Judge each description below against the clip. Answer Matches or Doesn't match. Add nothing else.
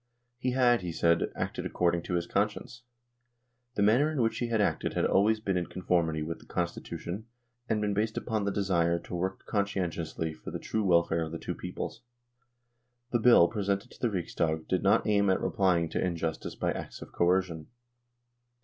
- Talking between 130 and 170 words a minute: Doesn't match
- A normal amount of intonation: Matches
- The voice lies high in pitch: Doesn't match